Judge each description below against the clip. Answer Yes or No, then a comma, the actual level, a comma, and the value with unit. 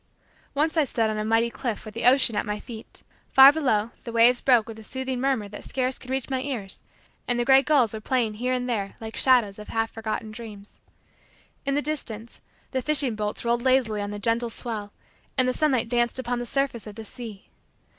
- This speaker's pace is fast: Yes, fast, 215 wpm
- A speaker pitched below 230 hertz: No, high, 235 Hz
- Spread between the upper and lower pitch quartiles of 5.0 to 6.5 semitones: No, average, 3.1 semitones